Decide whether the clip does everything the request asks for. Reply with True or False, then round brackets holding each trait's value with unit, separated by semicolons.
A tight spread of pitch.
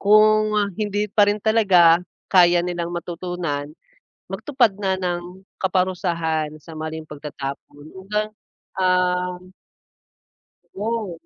False (3.3 semitones)